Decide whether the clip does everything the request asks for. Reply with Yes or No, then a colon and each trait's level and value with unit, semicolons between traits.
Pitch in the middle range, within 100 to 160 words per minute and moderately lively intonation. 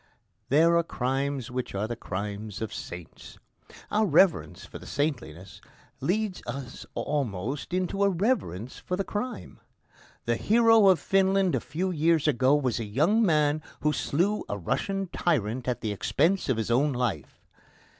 No: medium, 145 Hz; average, 155 wpm; wide, 8.0 semitones